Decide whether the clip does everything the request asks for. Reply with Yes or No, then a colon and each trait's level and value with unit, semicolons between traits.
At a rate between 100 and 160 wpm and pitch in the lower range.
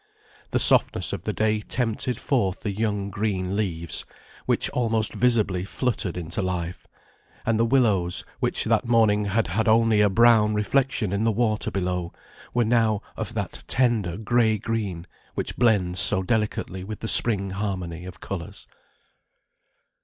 Yes: average, 150 wpm; low, 105 Hz